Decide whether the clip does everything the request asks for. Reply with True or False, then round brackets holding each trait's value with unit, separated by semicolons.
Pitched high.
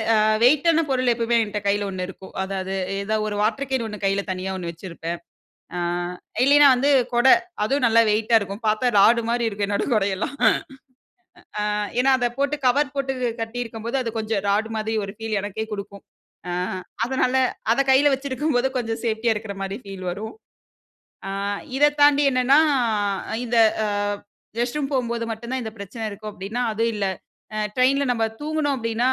True (225 Hz)